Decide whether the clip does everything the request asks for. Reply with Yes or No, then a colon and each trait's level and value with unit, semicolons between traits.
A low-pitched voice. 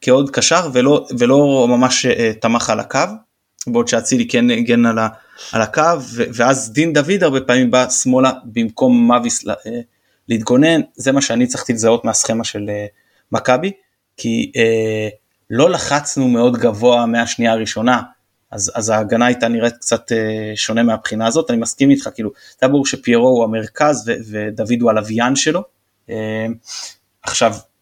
Yes: low, 120 Hz